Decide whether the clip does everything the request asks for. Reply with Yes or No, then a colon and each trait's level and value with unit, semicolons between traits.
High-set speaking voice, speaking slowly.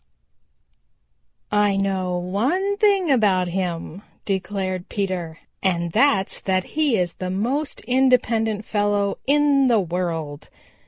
Yes: high, 200 Hz; slow, 110 wpm